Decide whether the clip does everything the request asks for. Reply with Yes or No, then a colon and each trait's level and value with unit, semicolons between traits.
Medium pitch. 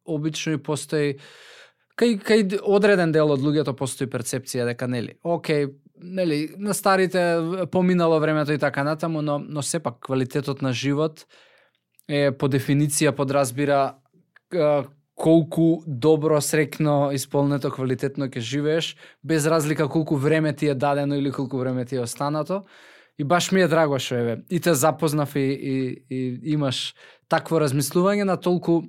Yes: medium, 150 Hz